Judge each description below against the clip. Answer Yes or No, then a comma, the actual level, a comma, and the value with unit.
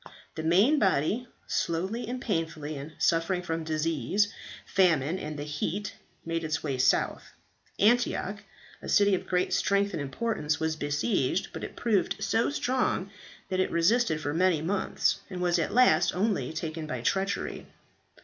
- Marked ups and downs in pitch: No, average, 4.5 semitones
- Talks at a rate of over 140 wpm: Yes, average, 155 wpm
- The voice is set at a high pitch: No, medium, 175 Hz